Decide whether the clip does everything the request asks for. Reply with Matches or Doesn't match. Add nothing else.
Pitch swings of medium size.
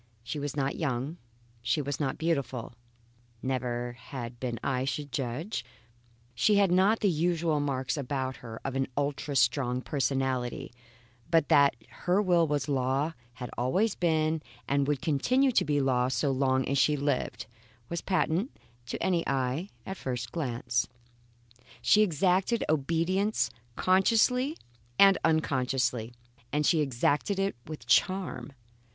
Matches